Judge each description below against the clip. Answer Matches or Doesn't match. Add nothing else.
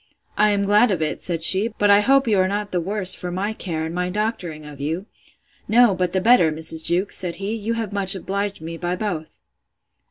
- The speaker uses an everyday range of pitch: Matches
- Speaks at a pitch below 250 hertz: Matches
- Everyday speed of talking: Doesn't match